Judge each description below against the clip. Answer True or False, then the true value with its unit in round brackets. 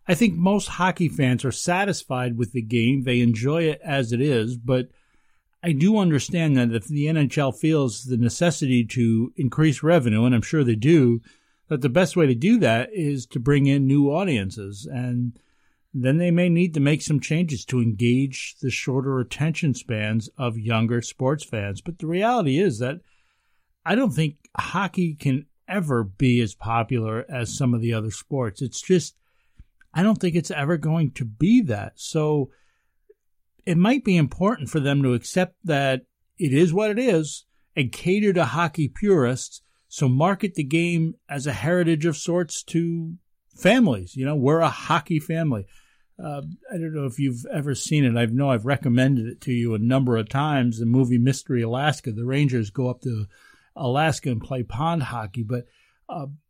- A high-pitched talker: False (140 Hz)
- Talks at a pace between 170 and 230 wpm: True (180 wpm)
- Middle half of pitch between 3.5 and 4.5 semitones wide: False (5.3 semitones)